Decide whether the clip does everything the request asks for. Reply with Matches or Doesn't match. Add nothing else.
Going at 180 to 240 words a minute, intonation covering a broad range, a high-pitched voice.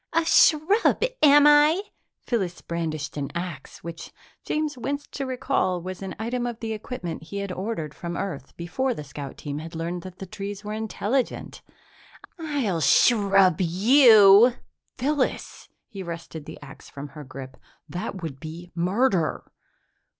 Doesn't match